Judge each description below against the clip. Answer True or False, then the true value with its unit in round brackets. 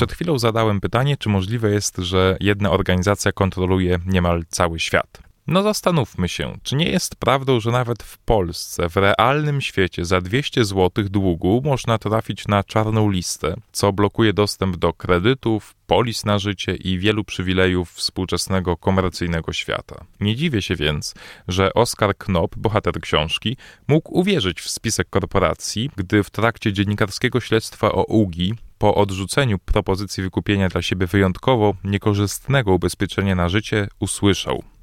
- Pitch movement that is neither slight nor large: True (3.2 semitones)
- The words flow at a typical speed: True (145 wpm)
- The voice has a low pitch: True (100 Hz)